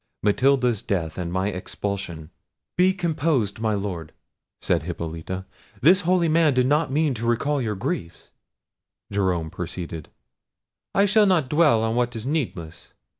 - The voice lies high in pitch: No, low, 110 Hz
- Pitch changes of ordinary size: No, wide, 8.5 semitones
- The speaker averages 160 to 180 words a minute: No, average, 140 wpm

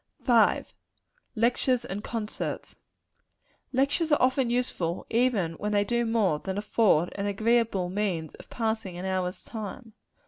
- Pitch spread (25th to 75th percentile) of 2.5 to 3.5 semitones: No, average, 3.9 semitones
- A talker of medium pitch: No, high, 215 Hz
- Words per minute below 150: Yes, average, 140 wpm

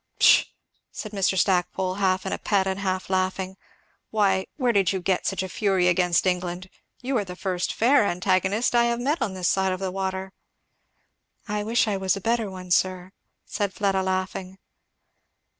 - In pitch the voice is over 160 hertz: Yes, high, 190 Hz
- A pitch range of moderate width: No, narrow, 1.7 semitones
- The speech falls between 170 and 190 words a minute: Yes, average, 180 wpm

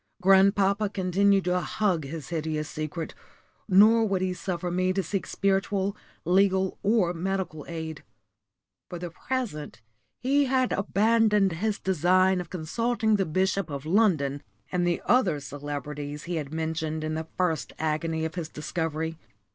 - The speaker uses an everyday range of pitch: Yes, average, 3.7 semitones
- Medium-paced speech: Yes, average, 145 wpm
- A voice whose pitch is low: No, medium, 180 Hz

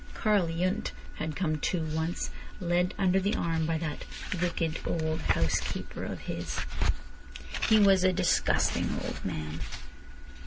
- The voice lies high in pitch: No, medium, 170 Hz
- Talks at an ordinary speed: No, slow, 130 wpm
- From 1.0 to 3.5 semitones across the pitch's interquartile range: Yes, average, 2.8 semitones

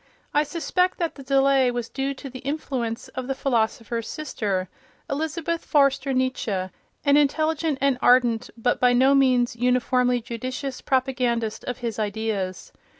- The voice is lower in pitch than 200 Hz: No, very high, 255 Hz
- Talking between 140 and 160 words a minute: Yes, average, 145 wpm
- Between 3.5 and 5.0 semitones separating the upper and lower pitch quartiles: No, average, 2.9 semitones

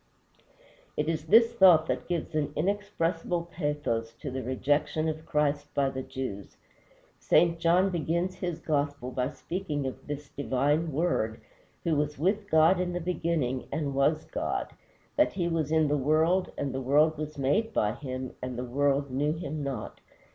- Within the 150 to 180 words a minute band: Yes, average, 170 wpm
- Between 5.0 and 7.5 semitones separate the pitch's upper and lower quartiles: No, average, 3.6 semitones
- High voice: No, medium, 150 Hz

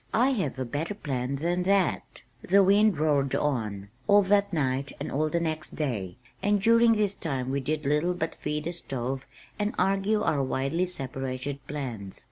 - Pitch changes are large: Yes, wide, 6.4 semitones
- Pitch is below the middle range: No, medium, 155 Hz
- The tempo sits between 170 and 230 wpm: Yes, average, 175 wpm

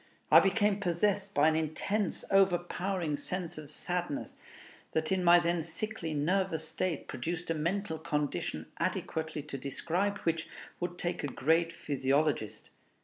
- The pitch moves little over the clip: No, average, 3.4 semitones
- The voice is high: No, medium, 170 Hz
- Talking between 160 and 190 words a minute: No, average, 140 wpm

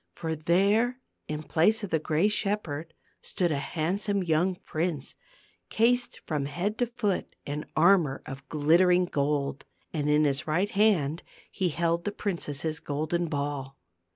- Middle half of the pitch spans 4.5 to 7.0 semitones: Yes, average, 4.8 semitones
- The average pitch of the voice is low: No, medium, 165 Hz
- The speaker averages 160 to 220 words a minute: No, average, 145 wpm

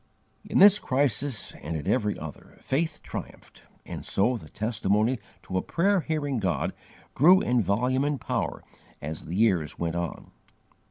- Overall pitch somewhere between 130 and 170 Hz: No, low, 115 Hz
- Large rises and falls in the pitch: Yes, wide, 7.5 semitones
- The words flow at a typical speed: Yes, average, 155 wpm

